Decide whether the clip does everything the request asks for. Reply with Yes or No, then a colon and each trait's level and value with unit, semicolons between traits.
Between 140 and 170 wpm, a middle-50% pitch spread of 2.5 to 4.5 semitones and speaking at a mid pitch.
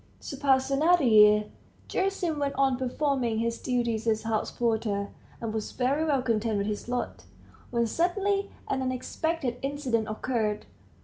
No: average, 145 wpm; average, 4.2 semitones; very high, 250 Hz